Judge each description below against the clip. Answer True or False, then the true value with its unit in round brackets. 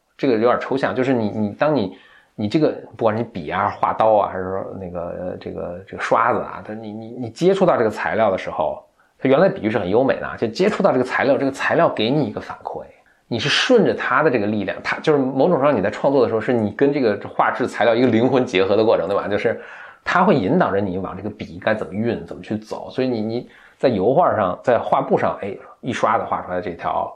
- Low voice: True (110 Hz)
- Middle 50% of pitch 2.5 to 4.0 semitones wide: False (4.6 semitones)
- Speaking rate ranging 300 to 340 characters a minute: False (360 characters per minute)